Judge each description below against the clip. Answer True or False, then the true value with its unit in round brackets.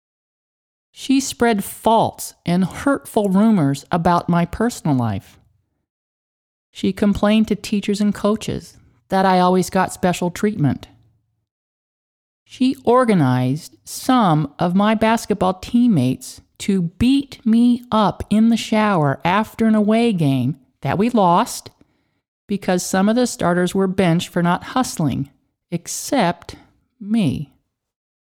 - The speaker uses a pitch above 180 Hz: True (190 Hz)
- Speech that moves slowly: True (115 wpm)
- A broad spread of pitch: True (7.0 semitones)